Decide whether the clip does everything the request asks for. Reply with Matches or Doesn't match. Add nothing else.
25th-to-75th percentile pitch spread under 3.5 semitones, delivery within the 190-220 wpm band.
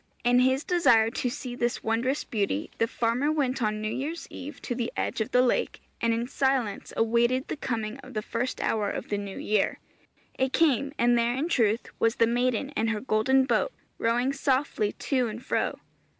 Matches